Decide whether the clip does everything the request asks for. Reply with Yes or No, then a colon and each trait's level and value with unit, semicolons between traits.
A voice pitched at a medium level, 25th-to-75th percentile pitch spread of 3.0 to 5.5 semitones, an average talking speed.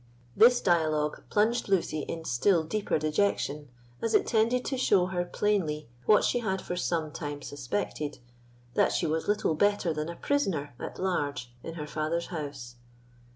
Yes: medium, 165 Hz; average, 5.2 semitones; average, 160 wpm